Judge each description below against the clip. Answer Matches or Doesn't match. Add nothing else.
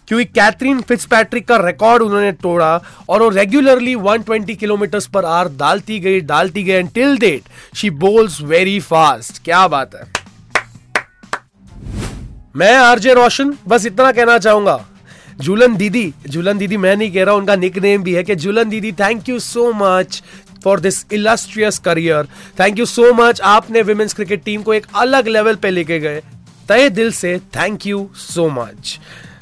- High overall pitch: Matches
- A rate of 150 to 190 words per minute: Matches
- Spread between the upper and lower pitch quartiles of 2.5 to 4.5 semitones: Matches